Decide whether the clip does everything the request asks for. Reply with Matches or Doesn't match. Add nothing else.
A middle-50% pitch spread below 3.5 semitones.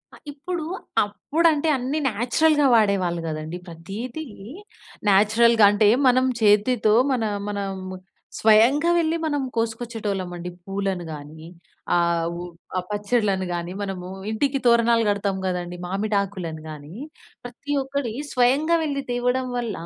Doesn't match